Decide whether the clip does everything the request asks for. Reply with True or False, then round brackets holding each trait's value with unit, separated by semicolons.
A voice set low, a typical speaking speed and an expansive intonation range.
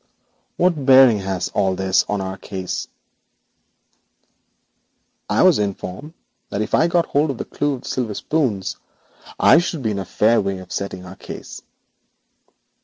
True (105 Hz; 165 wpm; 6.6 semitones)